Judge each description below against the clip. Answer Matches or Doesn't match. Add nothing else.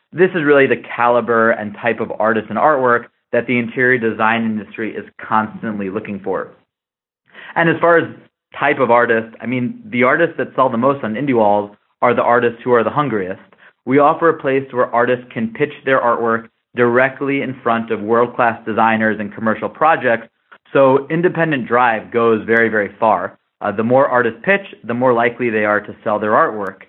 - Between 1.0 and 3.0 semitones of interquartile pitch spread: Matches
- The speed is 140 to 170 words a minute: Doesn't match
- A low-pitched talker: Matches